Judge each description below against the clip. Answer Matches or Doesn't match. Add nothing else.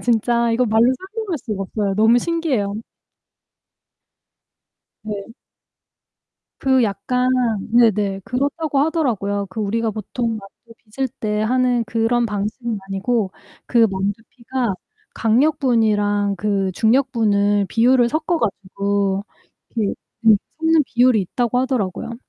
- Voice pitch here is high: Matches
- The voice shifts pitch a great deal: Doesn't match